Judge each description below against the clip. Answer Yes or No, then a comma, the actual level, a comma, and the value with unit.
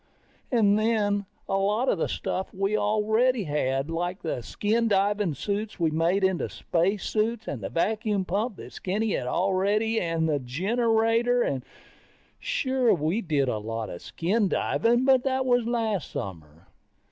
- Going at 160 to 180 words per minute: No, average, 150 wpm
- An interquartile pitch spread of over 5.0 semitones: Yes, wide, 5.4 semitones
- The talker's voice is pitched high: Yes, high, 200 Hz